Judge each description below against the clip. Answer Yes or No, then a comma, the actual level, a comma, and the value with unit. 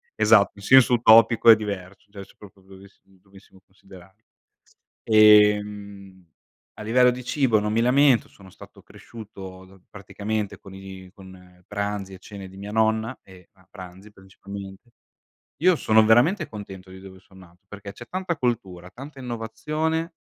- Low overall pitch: Yes, low, 100 Hz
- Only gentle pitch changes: No, average, 3.0 semitones